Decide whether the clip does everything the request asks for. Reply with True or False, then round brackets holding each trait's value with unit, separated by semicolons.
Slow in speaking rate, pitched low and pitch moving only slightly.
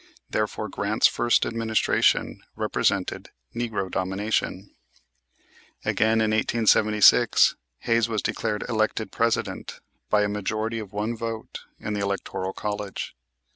True (110 wpm; 110 Hz; 1.6 semitones)